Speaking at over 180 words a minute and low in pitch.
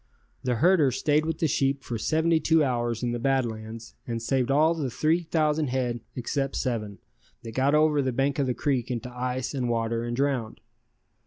Yes: average, 190 wpm; low, 130 Hz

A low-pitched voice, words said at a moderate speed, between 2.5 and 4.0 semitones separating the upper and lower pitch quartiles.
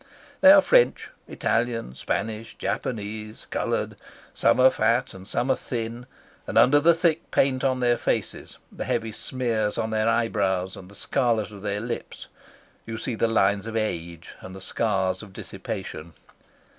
Yes: low, 110 Hz; average, 160 wpm; average, 3.5 semitones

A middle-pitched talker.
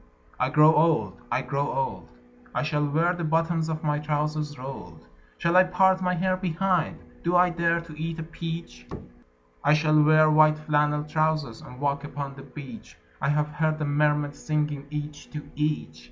Yes: medium, 150 Hz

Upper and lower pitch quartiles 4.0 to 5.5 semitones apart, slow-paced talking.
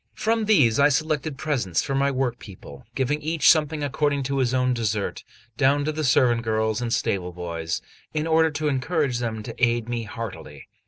No: average, 4.6 semitones; average, 180 wpm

